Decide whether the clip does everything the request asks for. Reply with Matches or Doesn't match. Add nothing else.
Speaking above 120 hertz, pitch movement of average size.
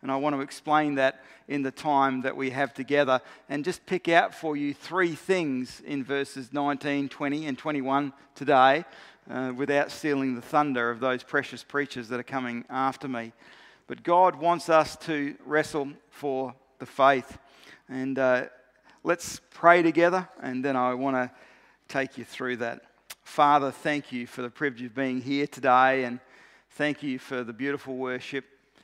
Doesn't match